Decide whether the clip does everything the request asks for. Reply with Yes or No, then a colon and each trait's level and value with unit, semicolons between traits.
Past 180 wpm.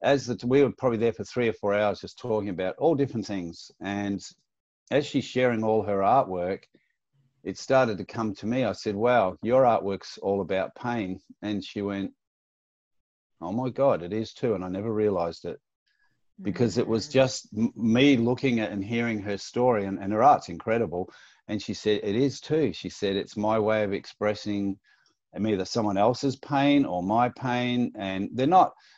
Yes: average, 190 wpm